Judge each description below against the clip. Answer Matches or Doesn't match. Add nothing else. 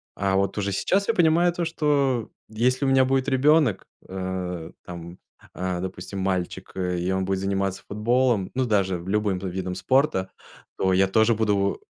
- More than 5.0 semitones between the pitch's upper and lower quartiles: Matches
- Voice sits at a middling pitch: Doesn't match